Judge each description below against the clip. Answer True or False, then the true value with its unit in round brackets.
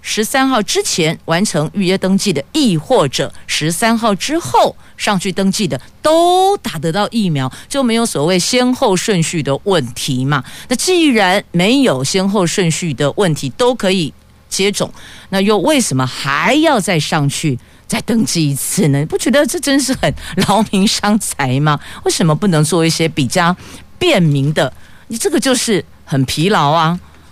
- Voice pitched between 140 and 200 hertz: True (190 Hz)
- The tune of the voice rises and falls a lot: True (7.1 semitones)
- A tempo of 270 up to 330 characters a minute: False (245 characters per minute)